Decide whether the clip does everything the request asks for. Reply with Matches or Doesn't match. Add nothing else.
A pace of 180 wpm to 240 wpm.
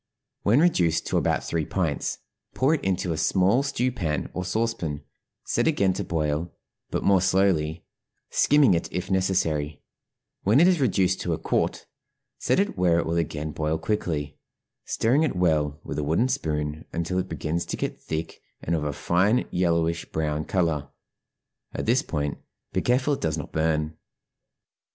Doesn't match